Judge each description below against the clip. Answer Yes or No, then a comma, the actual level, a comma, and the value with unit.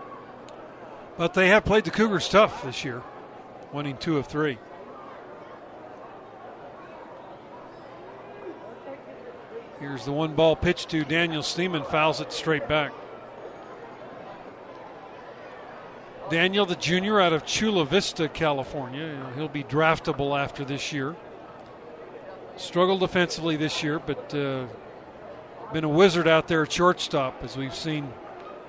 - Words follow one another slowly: Yes, slow, 115 wpm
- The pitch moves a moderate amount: Yes, average, 3.3 semitones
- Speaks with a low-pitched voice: No, medium, 155 Hz